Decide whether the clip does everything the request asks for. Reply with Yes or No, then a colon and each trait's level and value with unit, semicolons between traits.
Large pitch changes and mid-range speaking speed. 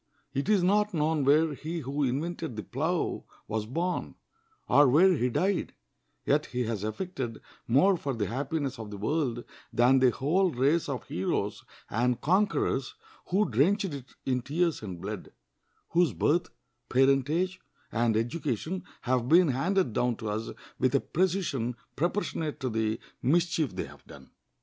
Yes: wide, 6.0 semitones; average, 155 wpm